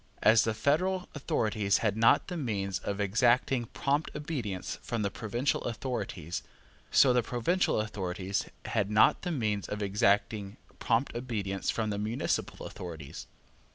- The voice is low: Yes, low, 110 Hz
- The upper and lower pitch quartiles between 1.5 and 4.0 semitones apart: Yes, average, 3.7 semitones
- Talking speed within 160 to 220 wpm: No, average, 140 wpm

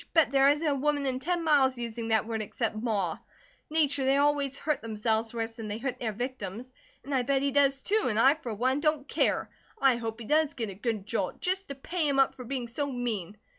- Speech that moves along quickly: Yes, fast, 235 wpm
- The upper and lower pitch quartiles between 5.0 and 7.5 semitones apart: No, average, 4.0 semitones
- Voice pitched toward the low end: No, very high, 260 Hz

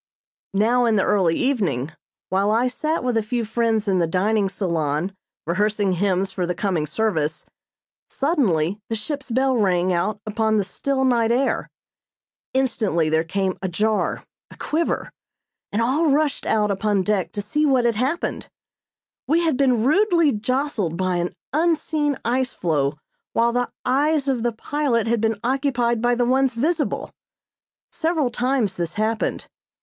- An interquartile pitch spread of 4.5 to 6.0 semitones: Yes, wide, 5.4 semitones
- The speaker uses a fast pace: No, average, 155 wpm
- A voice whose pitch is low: No, high, 225 Hz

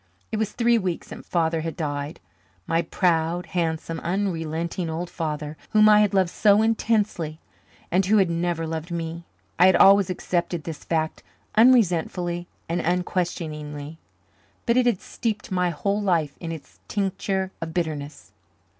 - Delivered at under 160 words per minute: Yes, average, 150 wpm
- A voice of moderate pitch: Yes, medium, 175 Hz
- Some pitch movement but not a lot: Yes, average, 3.3 semitones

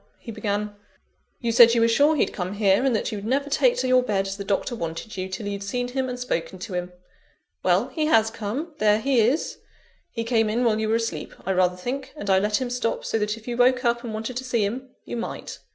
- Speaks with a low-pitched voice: No, high, 225 Hz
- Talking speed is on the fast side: Yes, fast, 250 wpm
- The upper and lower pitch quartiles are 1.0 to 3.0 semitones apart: No, average, 3.6 semitones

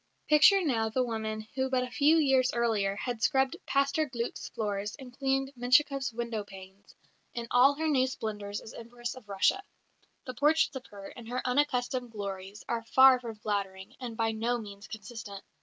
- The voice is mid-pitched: No, high, 240 Hz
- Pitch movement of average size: Yes, average, 3.6 semitones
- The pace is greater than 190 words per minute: No, average, 175 wpm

